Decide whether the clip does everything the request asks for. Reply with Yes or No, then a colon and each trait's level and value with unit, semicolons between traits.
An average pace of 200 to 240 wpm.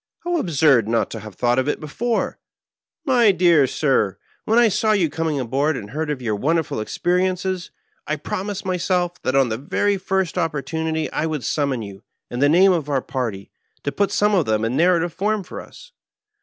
Yes: fast, 205 wpm